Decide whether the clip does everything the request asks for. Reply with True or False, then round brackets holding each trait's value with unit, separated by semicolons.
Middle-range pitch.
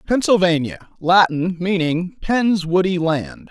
True (180 Hz)